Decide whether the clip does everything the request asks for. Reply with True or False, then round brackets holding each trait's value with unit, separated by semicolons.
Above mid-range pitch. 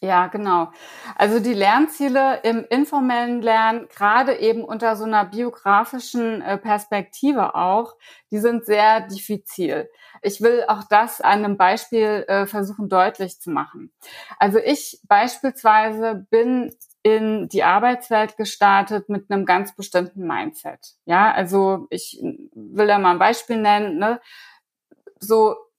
True (220 Hz)